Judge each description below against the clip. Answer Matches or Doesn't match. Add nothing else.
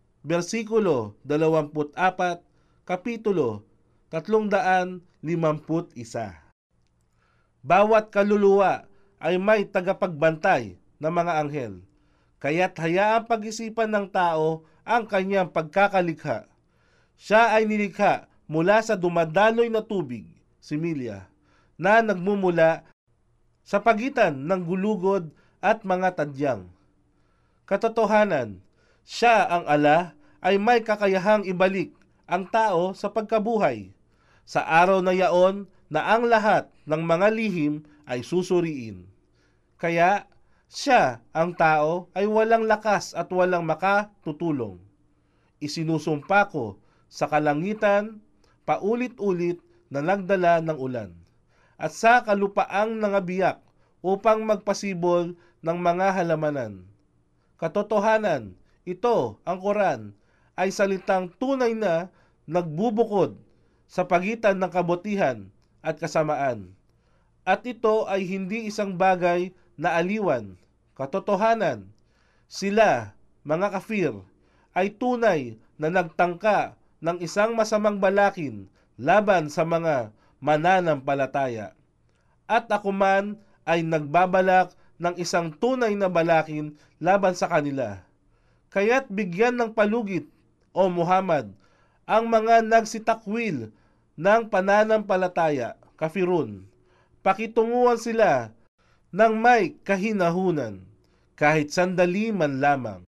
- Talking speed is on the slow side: Matches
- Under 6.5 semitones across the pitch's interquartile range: Matches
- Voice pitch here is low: Doesn't match